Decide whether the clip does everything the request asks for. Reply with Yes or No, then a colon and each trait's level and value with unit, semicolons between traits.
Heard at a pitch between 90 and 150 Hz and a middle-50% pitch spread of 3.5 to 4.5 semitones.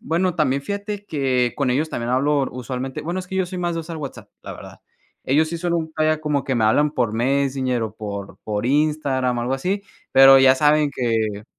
Yes: medium, 140 Hz; average, 4.0 semitones